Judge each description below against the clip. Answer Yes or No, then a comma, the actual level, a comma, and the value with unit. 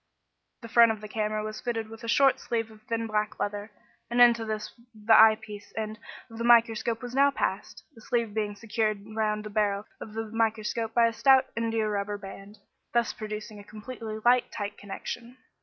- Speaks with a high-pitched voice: Yes, high, 220 Hz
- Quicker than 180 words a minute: Yes, average, 190 wpm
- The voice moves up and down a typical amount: No, narrow, 1.6 semitones